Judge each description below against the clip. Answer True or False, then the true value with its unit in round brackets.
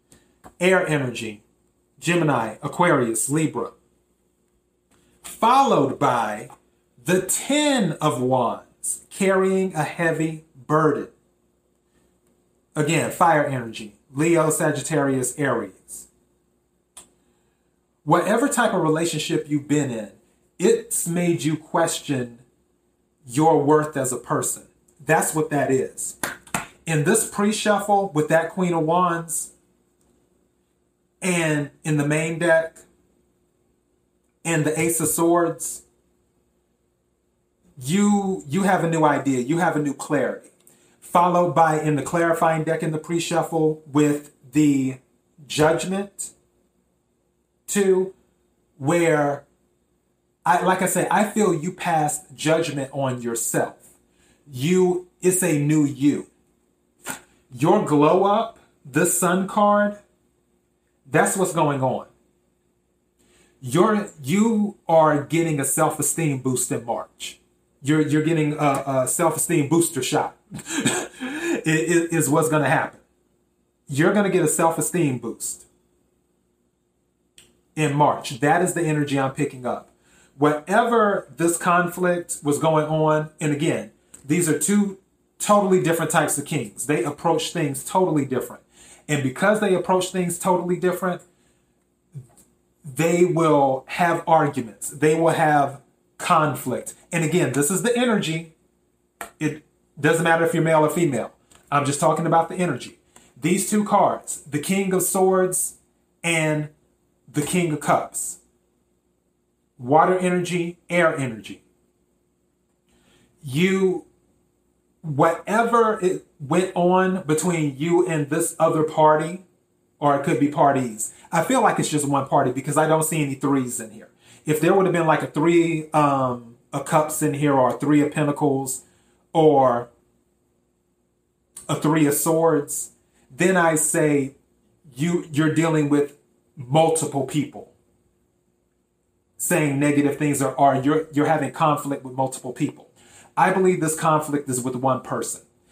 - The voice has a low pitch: False (150 Hz)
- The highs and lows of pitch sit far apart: True (5.8 semitones)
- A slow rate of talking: True (125 wpm)